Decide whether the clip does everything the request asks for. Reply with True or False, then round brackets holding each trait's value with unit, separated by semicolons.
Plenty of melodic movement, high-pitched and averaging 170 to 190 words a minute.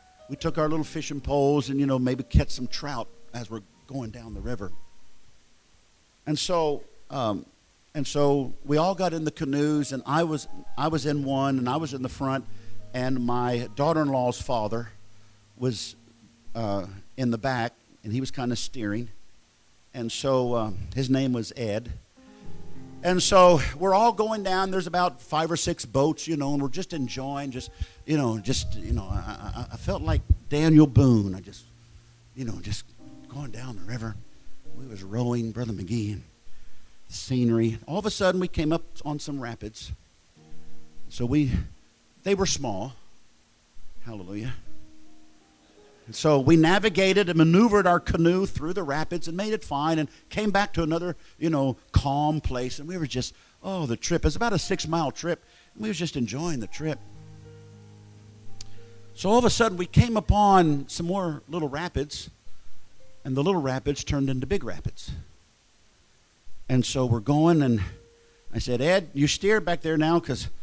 False (6.0 semitones; 130 Hz; 175 wpm)